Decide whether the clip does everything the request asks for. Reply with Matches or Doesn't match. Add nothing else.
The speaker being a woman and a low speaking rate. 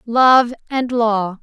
Matches